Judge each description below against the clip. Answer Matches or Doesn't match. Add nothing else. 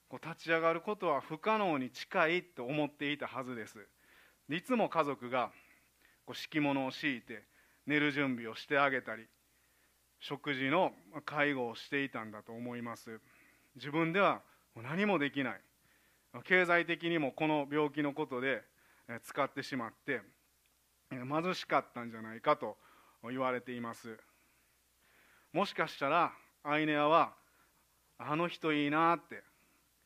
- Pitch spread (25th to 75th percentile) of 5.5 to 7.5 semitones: Doesn't match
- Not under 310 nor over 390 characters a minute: Doesn't match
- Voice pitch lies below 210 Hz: Matches